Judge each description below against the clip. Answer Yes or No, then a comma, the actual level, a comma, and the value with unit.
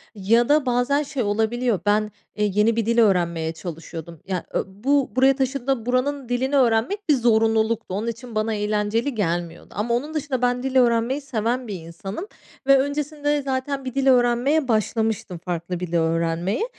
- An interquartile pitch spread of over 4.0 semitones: Yes, average, 4.5 semitones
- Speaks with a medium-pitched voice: No, high, 235 Hz